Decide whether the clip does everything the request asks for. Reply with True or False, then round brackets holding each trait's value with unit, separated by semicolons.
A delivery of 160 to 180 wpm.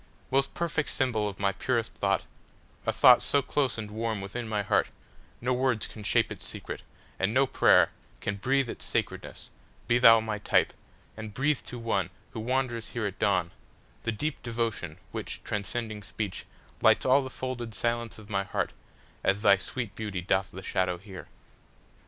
False (150 wpm)